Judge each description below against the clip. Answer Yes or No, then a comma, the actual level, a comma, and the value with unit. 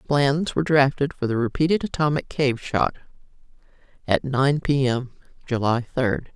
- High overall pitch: No, low, 135 Hz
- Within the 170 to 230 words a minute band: No, average, 140 wpm